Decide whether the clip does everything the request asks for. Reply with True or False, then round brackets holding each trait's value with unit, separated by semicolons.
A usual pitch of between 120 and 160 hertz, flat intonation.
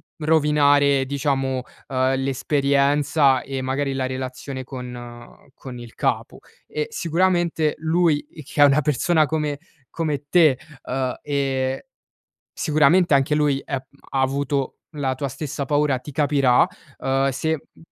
True (140 Hz; 2.1 semitones)